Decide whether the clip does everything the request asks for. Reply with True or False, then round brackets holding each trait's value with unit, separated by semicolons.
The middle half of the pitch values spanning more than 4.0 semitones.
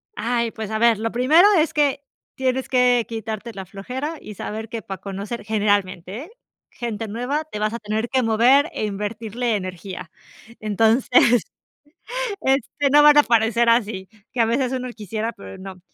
False (3.2 semitones)